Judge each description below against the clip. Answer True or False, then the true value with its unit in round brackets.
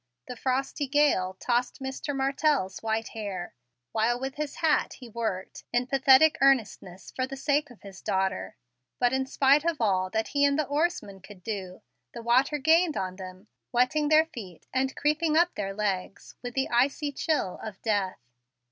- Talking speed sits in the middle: True (175 wpm)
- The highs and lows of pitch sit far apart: True (6.0 semitones)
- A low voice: False (250 Hz)